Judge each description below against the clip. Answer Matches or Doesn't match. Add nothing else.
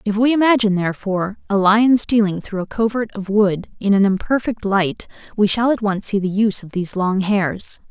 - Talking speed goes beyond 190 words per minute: Matches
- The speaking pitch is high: Matches